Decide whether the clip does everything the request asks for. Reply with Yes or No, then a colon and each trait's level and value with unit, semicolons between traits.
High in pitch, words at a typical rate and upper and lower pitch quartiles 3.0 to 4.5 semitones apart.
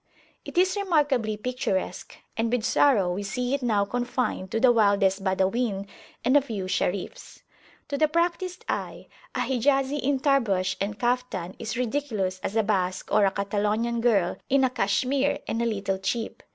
No: high, 230 Hz; average, 165 wpm; average, 5.0 semitones